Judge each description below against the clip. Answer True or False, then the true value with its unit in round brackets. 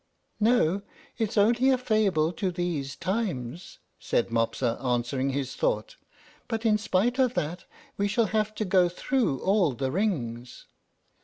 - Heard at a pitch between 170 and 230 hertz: True (185 Hz)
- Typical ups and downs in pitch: False (8.1 semitones)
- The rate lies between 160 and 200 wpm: False (145 wpm)